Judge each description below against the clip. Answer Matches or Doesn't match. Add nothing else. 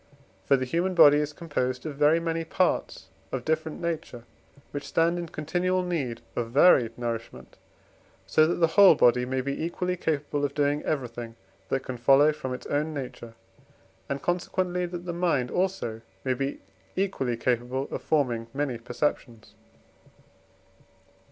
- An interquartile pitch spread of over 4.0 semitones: Matches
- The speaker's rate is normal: Matches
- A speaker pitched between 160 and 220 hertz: Doesn't match